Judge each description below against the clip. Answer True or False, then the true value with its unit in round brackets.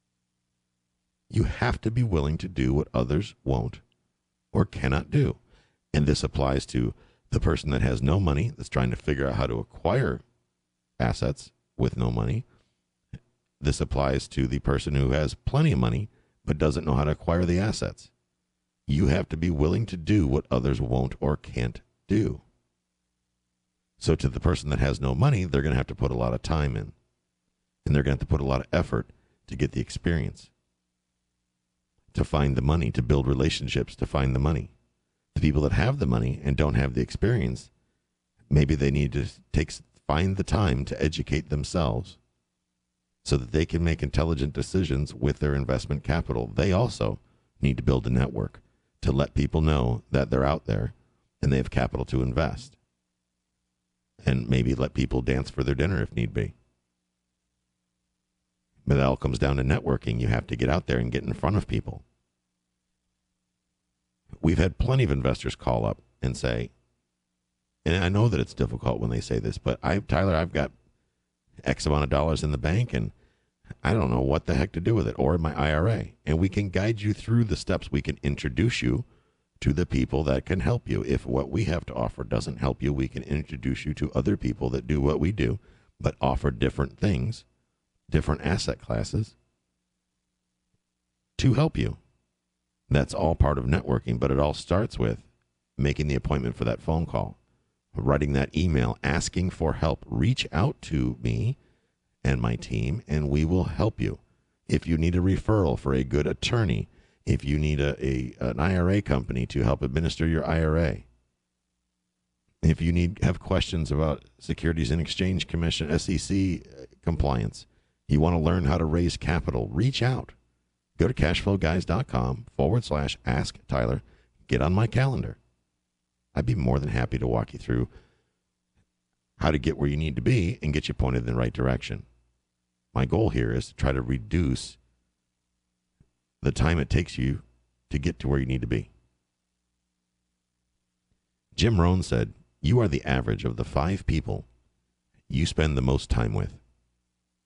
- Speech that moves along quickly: False (180 wpm)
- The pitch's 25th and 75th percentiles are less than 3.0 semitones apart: False (4.4 semitones)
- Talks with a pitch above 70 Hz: False (65 Hz)